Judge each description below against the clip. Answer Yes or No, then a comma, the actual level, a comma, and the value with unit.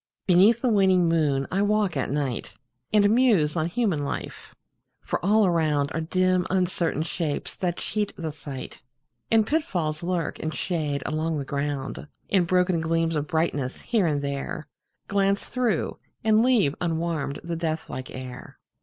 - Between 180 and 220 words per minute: No, average, 155 wpm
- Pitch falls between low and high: Yes, medium, 165 Hz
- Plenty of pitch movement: No, average, 4.5 semitones